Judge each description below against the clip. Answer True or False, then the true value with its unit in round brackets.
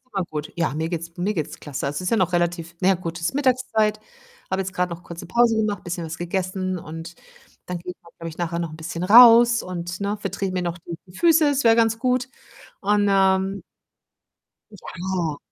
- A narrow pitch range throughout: False (3.7 semitones)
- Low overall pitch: False (185 Hz)